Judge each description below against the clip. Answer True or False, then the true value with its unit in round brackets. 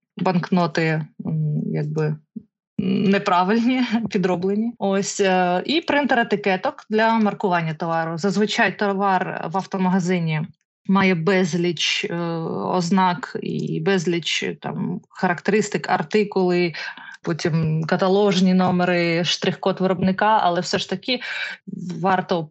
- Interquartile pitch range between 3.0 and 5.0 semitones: False (2.6 semitones)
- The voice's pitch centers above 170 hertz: True (190 Hz)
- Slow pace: True (90 wpm)